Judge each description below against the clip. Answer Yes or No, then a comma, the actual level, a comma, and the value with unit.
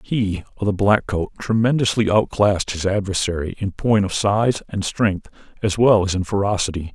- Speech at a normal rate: Yes, average, 175 wpm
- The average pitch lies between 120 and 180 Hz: No, low, 100 Hz